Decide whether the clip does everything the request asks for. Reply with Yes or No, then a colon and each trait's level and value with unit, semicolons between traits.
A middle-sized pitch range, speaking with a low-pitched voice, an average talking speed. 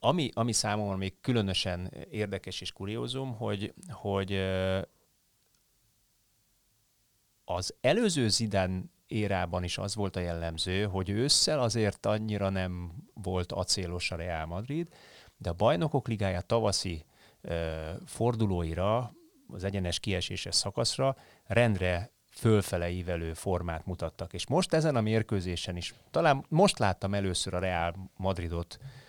Yes: average, 4.0 semitones; low, 100 Hz; average, 120 wpm